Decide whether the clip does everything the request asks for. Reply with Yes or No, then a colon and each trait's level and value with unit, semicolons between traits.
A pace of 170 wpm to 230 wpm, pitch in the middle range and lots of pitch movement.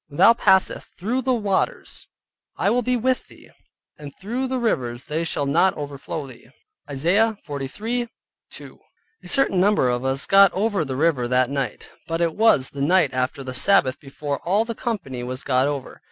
Yes: average, 180 wpm; medium, 165 Hz; wide, 8.1 semitones